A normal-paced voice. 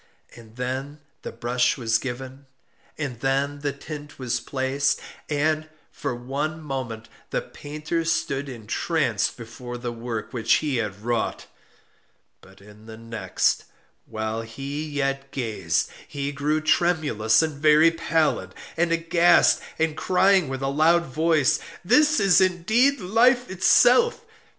No: slow, 130 wpm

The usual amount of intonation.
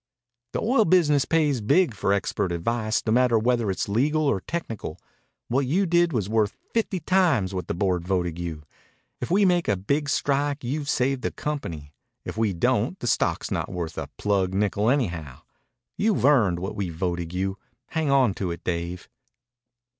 No: wide, 8.1 semitones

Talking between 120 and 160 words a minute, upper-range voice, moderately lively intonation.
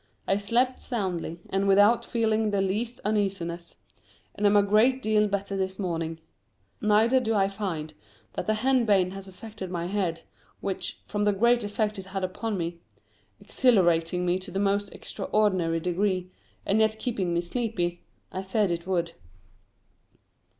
Yes: average, 155 wpm; high, 195 Hz; average, 3.1 semitones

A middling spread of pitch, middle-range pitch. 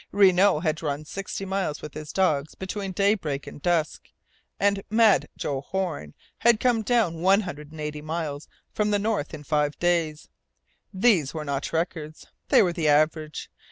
Yes: average, 4.5 semitones; medium, 165 Hz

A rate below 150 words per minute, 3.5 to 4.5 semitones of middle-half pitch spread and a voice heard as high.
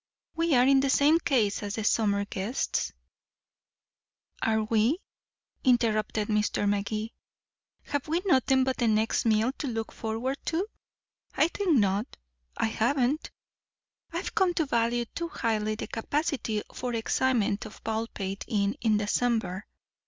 Yes: average, 140 wpm; average, 4.0 semitones; high, 230 Hz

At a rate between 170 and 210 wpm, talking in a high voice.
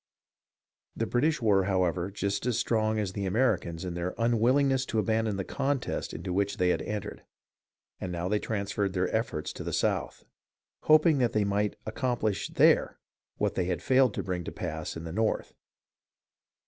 No: average, 175 wpm; low, 105 Hz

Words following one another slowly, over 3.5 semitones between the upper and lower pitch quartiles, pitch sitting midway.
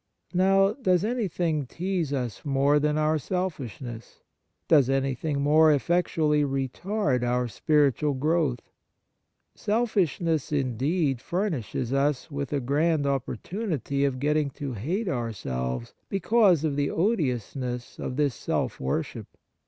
Yes: slow, 120 wpm; average, 4.7 semitones; medium, 145 Hz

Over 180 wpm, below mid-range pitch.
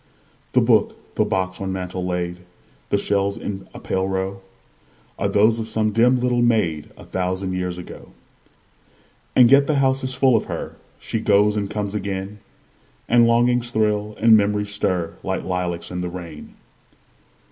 No: average, 165 wpm; low, 100 Hz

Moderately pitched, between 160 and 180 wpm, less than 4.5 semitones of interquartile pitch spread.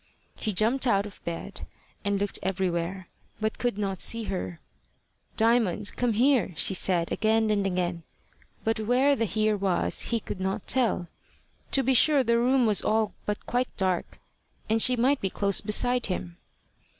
No: high, 215 Hz; average, 165 wpm; average, 3.9 semitones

